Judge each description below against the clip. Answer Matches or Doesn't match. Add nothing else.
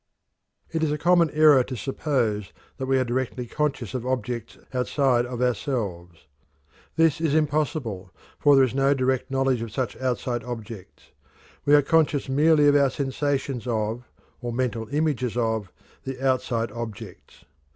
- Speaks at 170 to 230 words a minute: Doesn't match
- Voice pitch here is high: Doesn't match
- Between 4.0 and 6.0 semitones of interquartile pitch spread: Doesn't match